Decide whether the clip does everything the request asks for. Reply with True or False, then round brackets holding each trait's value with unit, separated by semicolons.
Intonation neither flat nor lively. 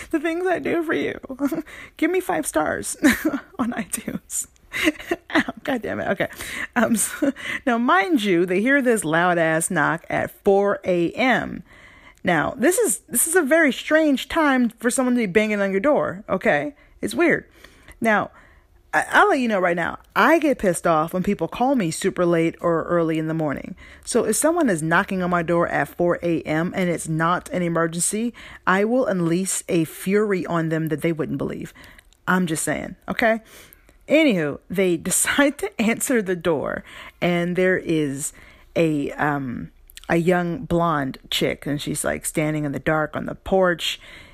False (8.1 semitones)